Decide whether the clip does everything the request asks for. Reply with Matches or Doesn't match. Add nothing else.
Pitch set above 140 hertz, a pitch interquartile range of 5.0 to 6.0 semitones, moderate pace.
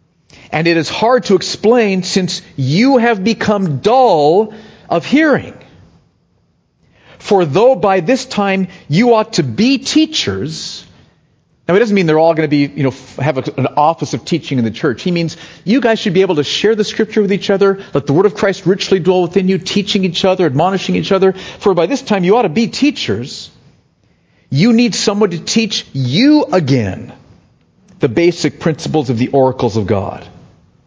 Matches